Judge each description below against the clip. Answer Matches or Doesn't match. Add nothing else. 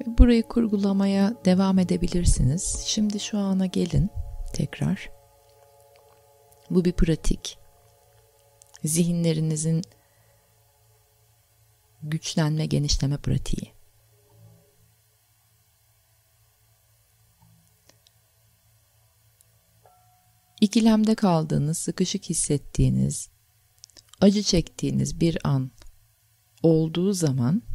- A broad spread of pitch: Matches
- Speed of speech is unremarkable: Doesn't match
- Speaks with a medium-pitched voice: Doesn't match